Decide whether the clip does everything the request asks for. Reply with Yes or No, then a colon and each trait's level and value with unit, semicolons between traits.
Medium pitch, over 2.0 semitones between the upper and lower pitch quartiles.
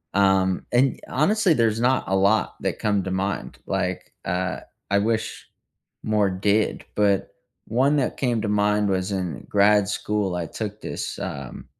No: low, 105 Hz; narrow, 2.5 semitones